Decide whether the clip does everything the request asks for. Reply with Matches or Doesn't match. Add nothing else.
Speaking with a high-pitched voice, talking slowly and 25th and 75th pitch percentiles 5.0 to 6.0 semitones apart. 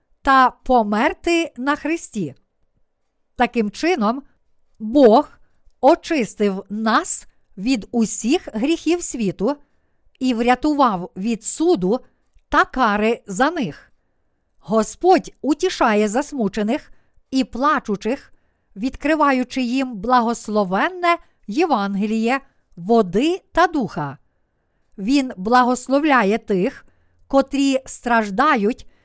Matches